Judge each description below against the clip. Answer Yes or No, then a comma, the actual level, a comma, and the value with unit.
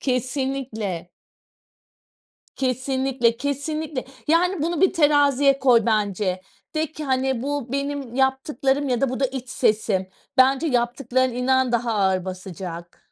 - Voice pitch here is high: Yes, very high, 260 Hz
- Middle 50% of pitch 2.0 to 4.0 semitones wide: Yes, average, 3.3 semitones